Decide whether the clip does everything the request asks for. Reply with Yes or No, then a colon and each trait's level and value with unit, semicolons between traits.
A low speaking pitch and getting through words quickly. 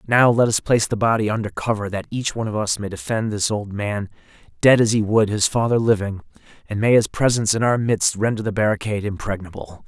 Yes: low, 105 Hz; fast, 220 wpm